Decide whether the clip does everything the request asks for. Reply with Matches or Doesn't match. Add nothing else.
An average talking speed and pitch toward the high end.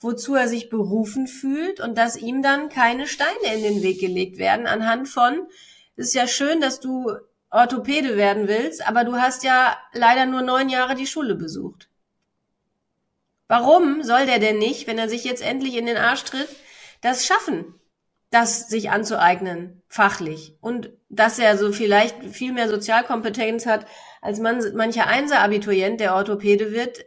Matches